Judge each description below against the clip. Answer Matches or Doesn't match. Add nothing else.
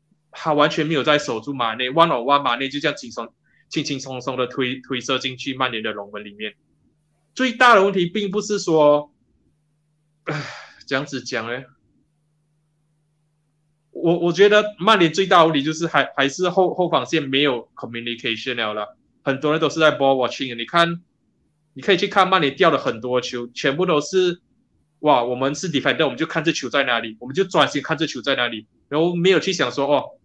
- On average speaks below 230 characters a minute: Doesn't match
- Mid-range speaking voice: Matches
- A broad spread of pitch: Doesn't match